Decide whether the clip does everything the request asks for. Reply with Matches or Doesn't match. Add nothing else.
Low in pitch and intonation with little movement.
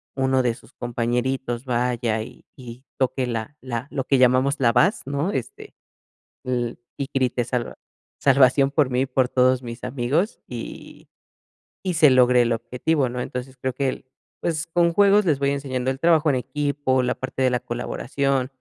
Matches